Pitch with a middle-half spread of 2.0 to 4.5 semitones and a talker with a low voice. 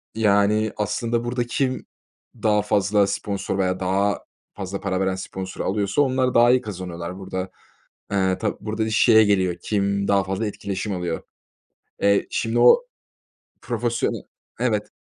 Yes: narrow, 2.5 semitones; low, 100 Hz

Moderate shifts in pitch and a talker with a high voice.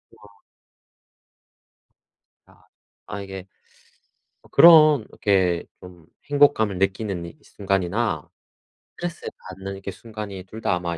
No: average, 3.2 semitones; low, 100 Hz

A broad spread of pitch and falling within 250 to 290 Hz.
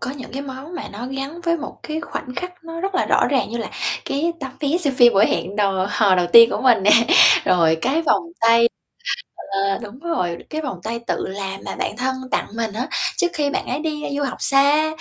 Yes: wide, 6.2 semitones; very high, 260 Hz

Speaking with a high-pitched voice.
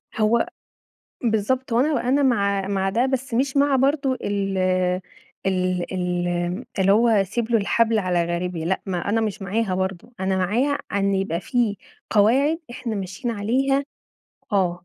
Yes: high, 205 Hz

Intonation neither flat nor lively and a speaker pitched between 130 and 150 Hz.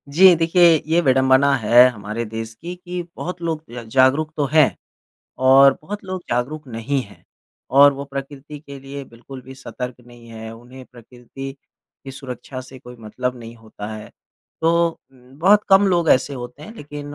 Yes: average, 4.1 semitones; low, 135 Hz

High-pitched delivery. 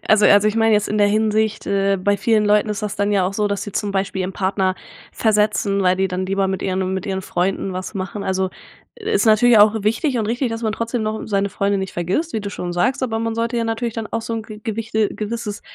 Yes: high, 210 Hz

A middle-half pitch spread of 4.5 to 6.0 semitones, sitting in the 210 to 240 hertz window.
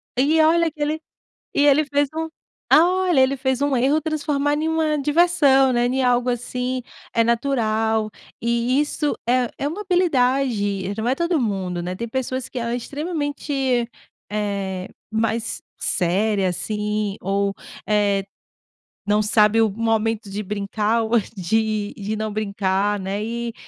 Yes: average, 5.1 semitones; high, 235 Hz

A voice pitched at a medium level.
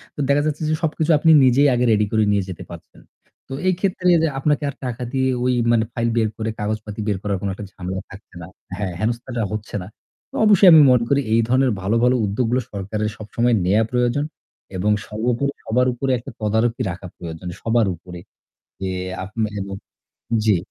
No: low, 115 Hz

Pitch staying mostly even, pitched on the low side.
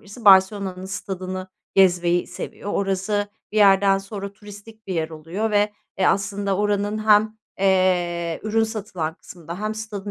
No: narrow, 2.0 semitones; high, 195 Hz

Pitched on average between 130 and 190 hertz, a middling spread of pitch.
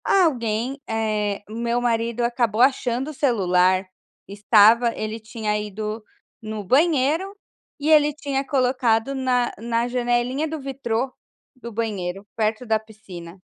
No: high, 235 Hz; average, 3.4 semitones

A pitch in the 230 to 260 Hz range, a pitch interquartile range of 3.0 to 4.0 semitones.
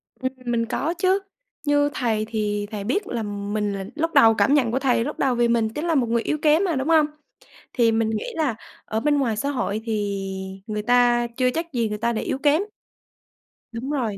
No: high, 240 Hz; average, 4.8 semitones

